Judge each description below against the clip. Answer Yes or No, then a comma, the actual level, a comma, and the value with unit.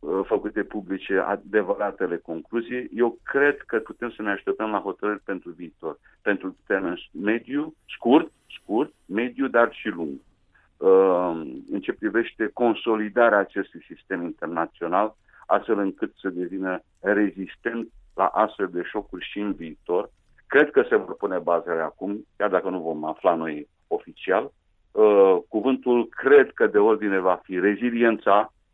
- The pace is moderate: Yes, average, 140 wpm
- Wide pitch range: Yes, wide, 6.9 semitones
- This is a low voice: Yes, low, 115 Hz